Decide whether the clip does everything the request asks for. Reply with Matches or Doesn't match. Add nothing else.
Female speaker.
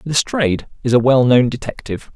Doesn't match